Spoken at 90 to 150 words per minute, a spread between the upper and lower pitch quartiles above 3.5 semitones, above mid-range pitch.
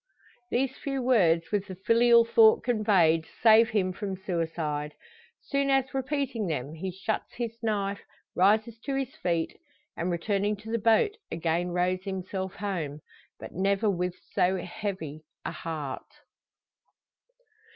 Yes: average, 140 wpm; average, 4.8 semitones; high, 195 Hz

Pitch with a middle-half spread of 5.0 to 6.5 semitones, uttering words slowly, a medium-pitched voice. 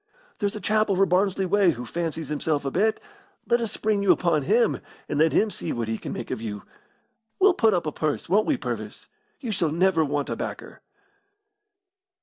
No: wide, 5.6 semitones; average, 200 wpm; medium, 180 Hz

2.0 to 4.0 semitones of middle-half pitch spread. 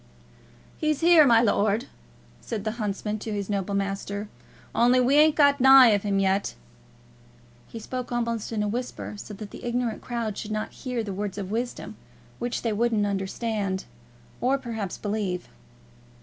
Yes: average, 3.1 semitones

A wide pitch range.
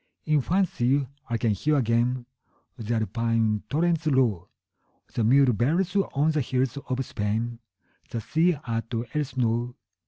No: average, 4.3 semitones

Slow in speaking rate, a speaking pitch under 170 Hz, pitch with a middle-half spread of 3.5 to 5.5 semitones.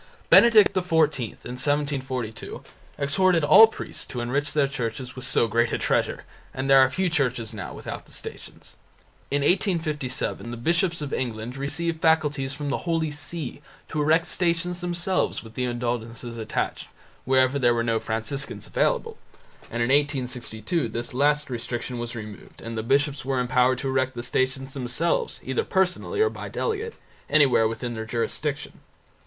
No: average, 160 wpm; low, 135 Hz; average, 4.7 semitones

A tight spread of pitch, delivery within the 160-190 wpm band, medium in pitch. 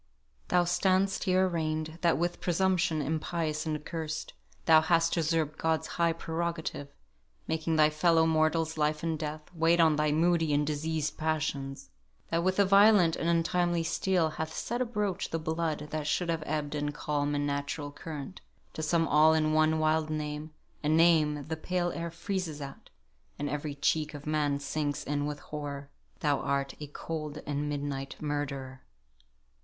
Yes: narrow, 2.0 semitones; average, 165 wpm; medium, 155 Hz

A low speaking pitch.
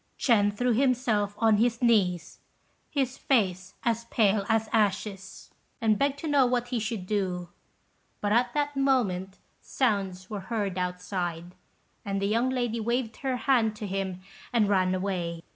No: high, 215 Hz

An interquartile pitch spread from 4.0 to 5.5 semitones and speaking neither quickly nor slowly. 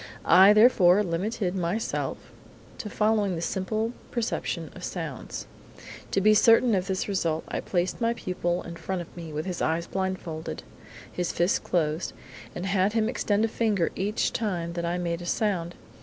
No: average, 3.5 semitones; average, 170 wpm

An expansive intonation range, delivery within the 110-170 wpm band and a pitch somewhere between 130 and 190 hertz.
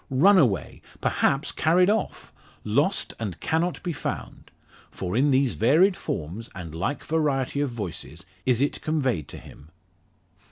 Yes: wide, 7.8 semitones; average, 145 wpm; low, 135 Hz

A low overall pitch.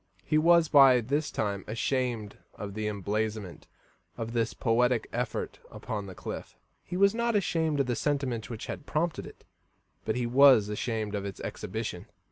Yes: low, 120 Hz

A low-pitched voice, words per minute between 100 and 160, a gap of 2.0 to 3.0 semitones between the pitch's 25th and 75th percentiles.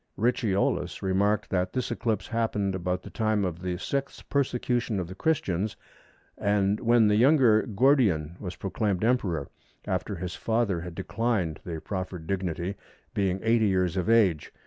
No: low, 100 Hz; average, 150 wpm; average, 4.0 semitones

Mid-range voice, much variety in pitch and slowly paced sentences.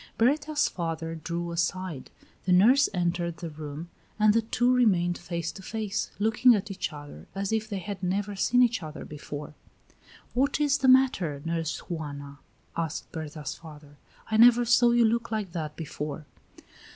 No: medium, 180 Hz; wide, 5.9 semitones; average, 165 wpm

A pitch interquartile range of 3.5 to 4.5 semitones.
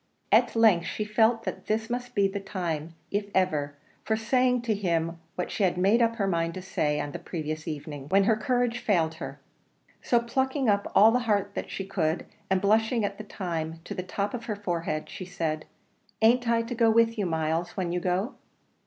No: average, 5.2 semitones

